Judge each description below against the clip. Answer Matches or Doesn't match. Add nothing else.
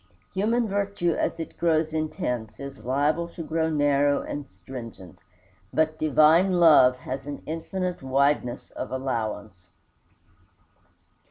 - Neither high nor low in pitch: Matches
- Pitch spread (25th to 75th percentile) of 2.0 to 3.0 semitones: Doesn't match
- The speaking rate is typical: Doesn't match